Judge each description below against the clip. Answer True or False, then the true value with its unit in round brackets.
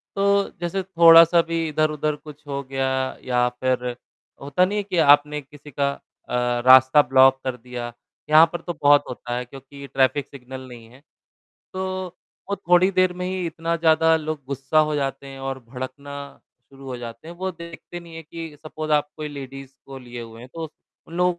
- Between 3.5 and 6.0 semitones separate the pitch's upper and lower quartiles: True (4.0 semitones)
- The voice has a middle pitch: True (145 Hz)